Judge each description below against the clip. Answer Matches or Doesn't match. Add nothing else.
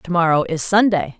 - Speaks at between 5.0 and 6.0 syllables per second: Matches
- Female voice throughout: Matches